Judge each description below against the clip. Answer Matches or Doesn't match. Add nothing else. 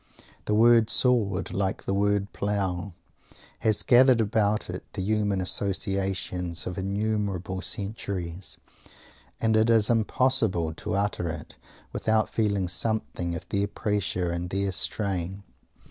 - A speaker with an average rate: Doesn't match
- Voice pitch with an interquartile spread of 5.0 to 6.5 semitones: Doesn't match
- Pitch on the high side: Doesn't match